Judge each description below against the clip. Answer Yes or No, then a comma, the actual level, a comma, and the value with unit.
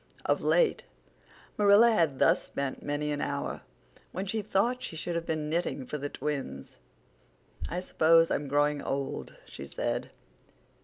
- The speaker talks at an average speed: Yes, average, 150 wpm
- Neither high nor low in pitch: Yes, medium, 160 Hz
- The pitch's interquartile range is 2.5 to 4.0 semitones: No, average, 4.9 semitones